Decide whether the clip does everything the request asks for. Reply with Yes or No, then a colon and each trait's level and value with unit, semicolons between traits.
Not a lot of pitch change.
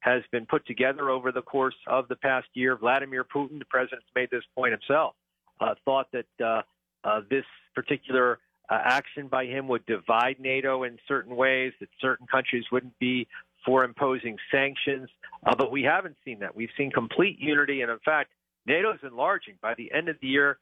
Yes: narrow, 1.7 semitones